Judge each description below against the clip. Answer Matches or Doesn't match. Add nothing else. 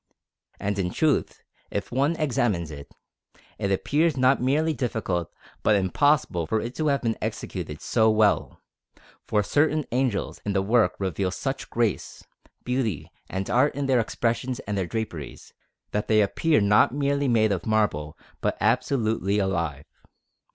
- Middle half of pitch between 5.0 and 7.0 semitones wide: Matches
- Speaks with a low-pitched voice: Matches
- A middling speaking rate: Matches